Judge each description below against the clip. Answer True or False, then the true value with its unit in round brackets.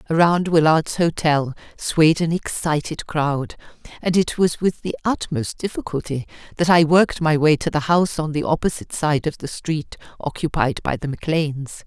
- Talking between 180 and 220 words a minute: False (165 wpm)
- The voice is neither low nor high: True (155 Hz)